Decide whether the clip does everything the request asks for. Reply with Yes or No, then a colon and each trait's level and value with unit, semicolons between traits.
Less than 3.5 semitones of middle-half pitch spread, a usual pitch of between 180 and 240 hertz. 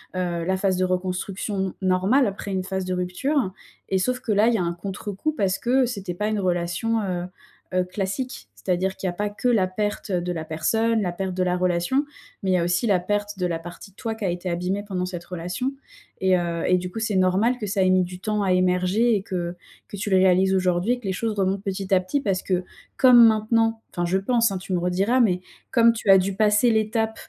Yes: average, 2.9 semitones; high, 190 Hz